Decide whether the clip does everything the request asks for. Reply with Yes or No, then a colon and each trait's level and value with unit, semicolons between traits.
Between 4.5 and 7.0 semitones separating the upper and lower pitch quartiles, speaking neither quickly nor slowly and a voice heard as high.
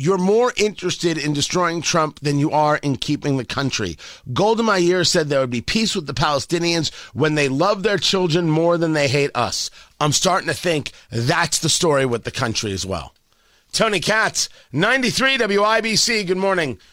No: average, 5.2 semitones; average, 180 wpm; medium, 160 Hz